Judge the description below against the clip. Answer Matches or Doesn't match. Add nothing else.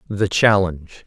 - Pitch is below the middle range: Matches